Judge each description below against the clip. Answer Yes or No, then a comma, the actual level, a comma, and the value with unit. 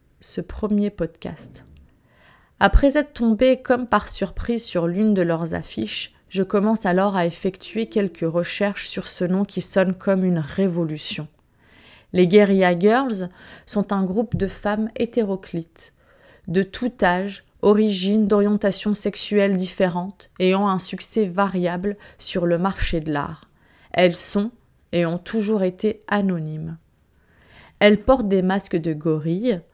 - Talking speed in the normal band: No, slow, 135 wpm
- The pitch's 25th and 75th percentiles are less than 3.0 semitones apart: No, average, 3.3 semitones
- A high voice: Yes, high, 195 Hz